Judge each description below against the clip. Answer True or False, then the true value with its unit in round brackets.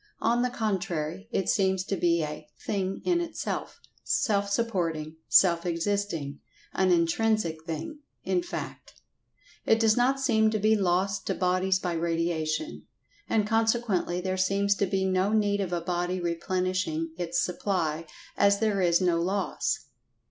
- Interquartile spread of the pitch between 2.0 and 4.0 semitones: True (3.7 semitones)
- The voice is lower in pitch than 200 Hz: True (190 Hz)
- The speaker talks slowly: False (145 wpm)